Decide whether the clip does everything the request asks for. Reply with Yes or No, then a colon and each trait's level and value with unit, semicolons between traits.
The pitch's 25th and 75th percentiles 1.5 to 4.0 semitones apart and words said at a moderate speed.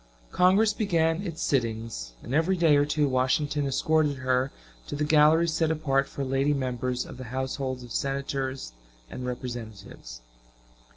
Yes: average, 3.7 semitones; average, 150 wpm